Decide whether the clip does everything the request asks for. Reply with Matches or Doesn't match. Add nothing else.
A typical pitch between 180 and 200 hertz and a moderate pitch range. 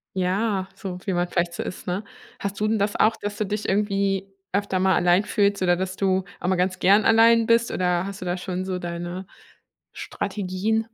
Doesn't match